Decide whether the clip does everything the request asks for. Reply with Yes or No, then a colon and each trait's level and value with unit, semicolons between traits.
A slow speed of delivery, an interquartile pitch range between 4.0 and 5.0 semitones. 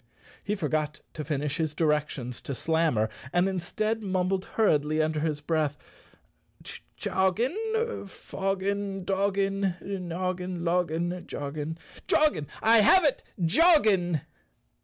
Yes: slow, 115 wpm; average, 4.4 semitones